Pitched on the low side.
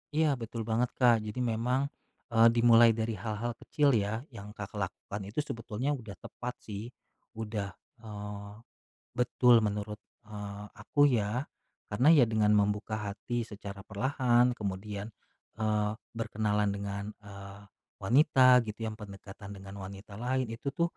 Yes: low, 110 Hz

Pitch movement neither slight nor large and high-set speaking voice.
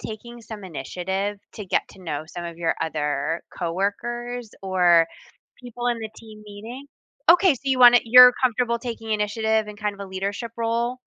Yes: average, 4.2 semitones; high, 215 Hz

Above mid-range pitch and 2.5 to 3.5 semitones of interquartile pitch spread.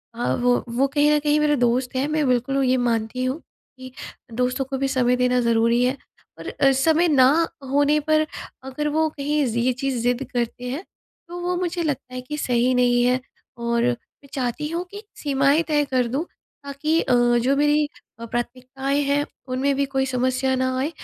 Yes: very high, 265 Hz; average, 3.0 semitones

